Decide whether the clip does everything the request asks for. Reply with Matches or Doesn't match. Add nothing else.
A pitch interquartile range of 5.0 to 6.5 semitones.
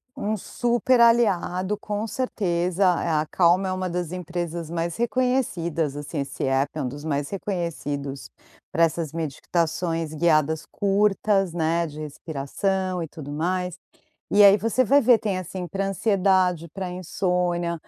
Doesn't match